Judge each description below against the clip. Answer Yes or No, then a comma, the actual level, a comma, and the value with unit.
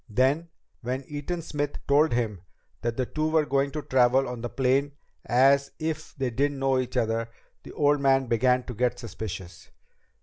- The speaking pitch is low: Yes, low, 130 Hz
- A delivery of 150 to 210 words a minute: Yes, average, 175 wpm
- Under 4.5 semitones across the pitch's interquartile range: Yes, average, 2.8 semitones